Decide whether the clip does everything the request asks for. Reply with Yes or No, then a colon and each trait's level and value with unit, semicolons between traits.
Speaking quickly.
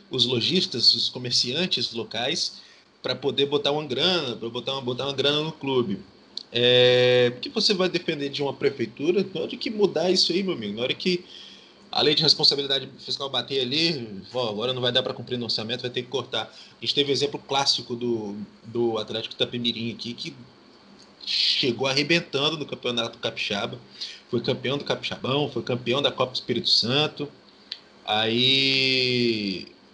No: average, 175 wpm